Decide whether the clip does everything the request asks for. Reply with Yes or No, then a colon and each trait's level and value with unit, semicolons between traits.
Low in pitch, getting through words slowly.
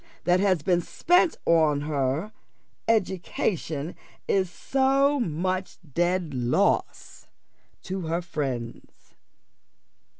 No: medium, 175 Hz; slow, 90 wpm